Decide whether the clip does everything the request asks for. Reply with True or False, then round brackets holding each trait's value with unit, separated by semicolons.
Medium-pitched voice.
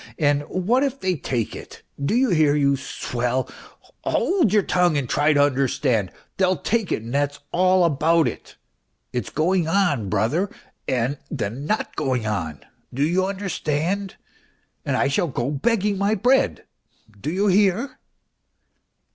True (155 Hz)